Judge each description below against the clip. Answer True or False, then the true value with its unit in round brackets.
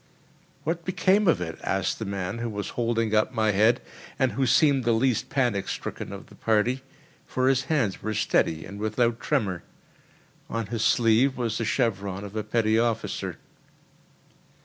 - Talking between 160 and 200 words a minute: True (170 wpm)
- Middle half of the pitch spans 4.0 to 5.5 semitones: False (3.5 semitones)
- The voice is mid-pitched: False (115 Hz)